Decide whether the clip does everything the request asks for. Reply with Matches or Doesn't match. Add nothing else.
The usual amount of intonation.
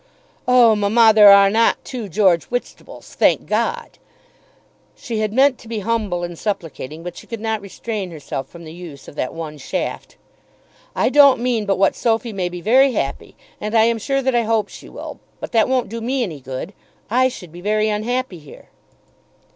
Matches